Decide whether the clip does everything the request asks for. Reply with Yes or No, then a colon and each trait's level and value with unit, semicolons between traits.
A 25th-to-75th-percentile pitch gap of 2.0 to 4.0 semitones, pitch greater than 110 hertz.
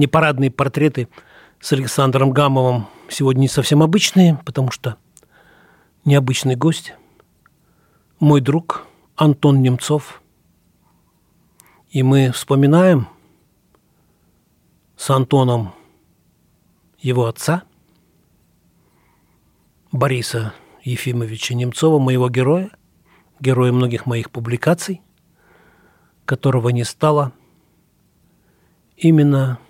Yes: average, 3.1 semitones; low, 135 Hz